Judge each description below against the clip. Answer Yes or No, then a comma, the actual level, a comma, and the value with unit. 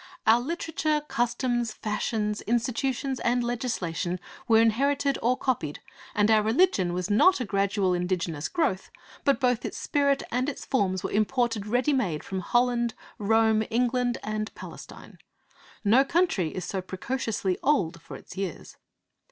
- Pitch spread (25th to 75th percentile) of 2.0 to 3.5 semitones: No, average, 4.4 semitones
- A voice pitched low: No, high, 225 Hz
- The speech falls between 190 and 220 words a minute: No, average, 145 wpm